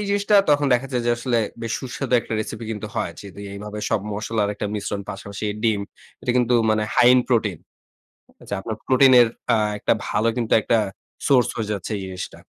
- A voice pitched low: Yes, low, 115 Hz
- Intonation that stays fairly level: No, average, 3.2 semitones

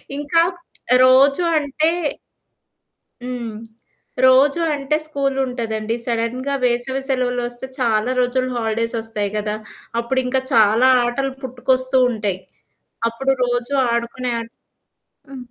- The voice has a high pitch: Yes, very high, 250 Hz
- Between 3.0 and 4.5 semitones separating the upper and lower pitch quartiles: No, narrow, 2.5 semitones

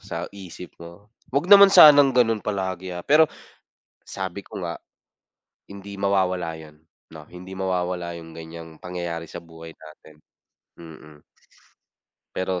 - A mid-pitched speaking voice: No, very low, 90 Hz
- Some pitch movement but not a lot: Yes, average, 3.2 semitones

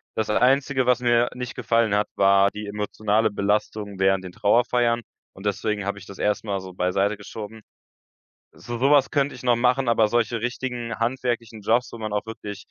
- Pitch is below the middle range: Yes, low, 110 Hz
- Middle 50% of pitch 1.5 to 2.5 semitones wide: No, average, 2.9 semitones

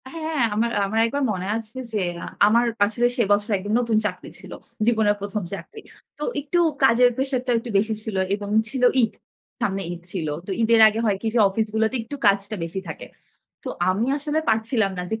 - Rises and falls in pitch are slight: No, average, 3.1 semitones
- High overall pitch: Yes, high, 220 Hz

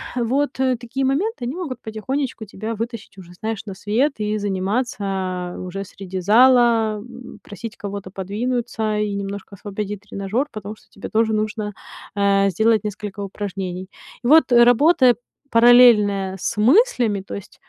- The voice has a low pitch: No, high, 215 Hz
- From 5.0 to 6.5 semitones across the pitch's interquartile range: No, average, 3.5 semitones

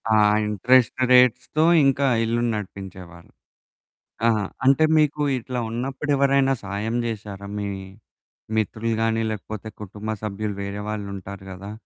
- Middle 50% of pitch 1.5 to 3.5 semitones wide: No, average, 4.1 semitones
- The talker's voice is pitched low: Yes, low, 110 Hz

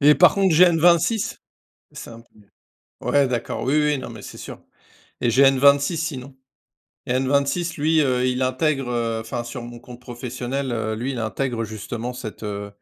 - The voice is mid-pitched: No, low, 130 Hz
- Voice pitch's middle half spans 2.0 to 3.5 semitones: Yes, average, 3.2 semitones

